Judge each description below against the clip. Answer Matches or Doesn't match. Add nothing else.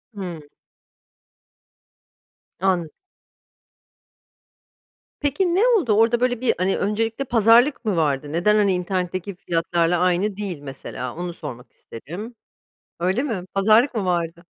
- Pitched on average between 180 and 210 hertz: Matches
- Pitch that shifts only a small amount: Doesn't match